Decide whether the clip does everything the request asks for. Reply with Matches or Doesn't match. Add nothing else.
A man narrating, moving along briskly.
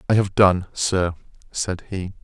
Doesn't match